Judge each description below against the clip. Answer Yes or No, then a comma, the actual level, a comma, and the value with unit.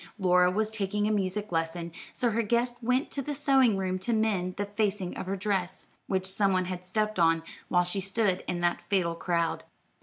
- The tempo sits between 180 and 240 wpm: Yes, fast, 205 wpm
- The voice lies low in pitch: No, high, 195 Hz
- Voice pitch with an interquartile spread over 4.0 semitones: No, average, 3.1 semitones